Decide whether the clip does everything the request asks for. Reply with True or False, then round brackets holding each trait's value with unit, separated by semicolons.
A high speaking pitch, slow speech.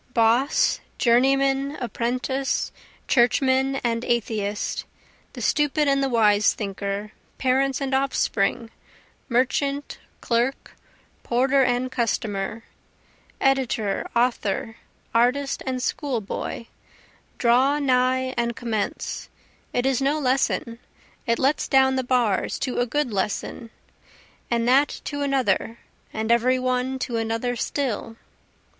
True (250 Hz; 110 wpm)